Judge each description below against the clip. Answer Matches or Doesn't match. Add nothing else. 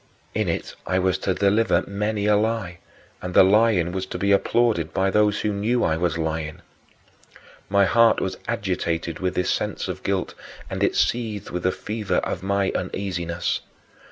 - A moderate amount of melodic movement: Matches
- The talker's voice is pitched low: Matches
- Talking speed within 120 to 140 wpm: Doesn't match